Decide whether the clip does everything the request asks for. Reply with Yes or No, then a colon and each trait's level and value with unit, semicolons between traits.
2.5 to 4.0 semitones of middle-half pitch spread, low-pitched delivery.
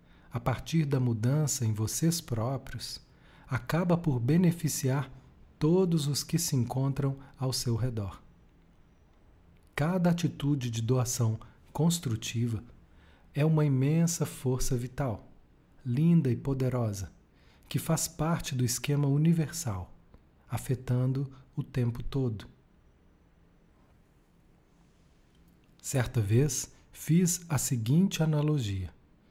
No: average, 4.4 semitones; low, 130 Hz